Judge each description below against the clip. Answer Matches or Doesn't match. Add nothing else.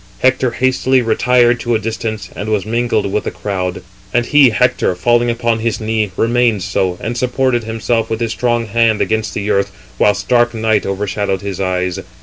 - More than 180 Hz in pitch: Doesn't match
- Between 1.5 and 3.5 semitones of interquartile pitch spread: Matches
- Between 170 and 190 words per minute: Matches